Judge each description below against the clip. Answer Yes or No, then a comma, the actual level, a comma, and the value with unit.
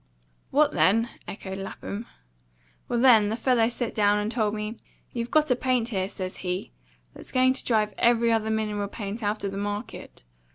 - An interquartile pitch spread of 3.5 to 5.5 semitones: No, narrow, 2.5 semitones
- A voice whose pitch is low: No, high, 220 Hz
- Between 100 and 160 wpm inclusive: No, average, 180 wpm